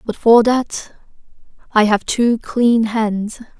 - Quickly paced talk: No, slow, 135 wpm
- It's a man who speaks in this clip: No, female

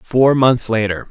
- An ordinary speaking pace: Yes, average, 160 wpm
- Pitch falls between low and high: No, low, 120 Hz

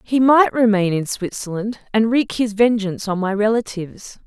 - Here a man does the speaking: No, female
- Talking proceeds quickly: No, average, 170 wpm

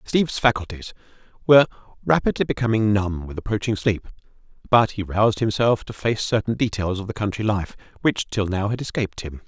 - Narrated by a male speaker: Yes, male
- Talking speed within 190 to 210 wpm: No, average, 170 wpm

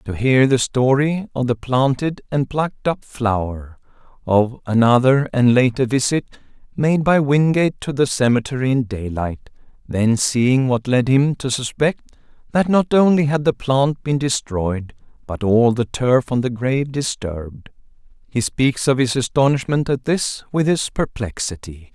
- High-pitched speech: No, low, 130 Hz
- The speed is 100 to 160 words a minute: Yes, average, 155 wpm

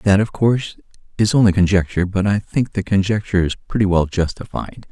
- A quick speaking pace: No, average, 185 wpm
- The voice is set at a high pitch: No, low, 100 Hz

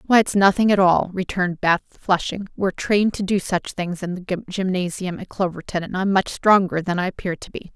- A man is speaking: No, female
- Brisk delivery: Yes, fast, 215 wpm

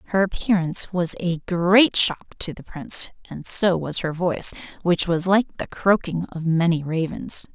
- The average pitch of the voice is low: No, medium, 175 Hz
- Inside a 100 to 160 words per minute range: No, average, 175 wpm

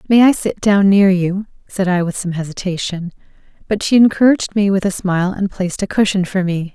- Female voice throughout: Yes, female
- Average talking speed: No, fast, 215 wpm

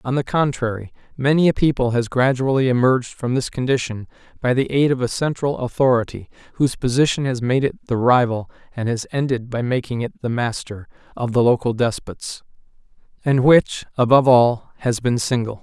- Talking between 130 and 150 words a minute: No, average, 175 wpm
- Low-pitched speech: Yes, low, 125 Hz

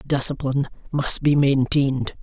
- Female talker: Yes, female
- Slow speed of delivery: Yes, slow, 110 wpm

